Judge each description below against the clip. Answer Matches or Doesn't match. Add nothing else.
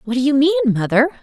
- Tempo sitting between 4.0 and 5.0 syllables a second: Doesn't match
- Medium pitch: Doesn't match